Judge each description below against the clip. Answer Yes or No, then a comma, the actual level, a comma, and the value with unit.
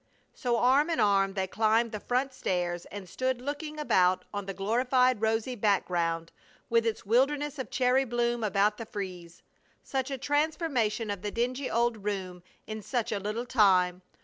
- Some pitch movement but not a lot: Yes, average, 4.5 semitones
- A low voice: No, high, 225 Hz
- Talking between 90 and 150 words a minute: No, average, 170 wpm